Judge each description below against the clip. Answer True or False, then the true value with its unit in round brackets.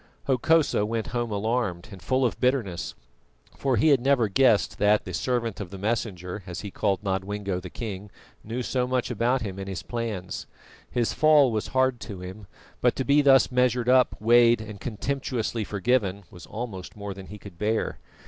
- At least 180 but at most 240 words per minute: True (185 wpm)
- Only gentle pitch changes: False (4.2 semitones)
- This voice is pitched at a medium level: False (110 Hz)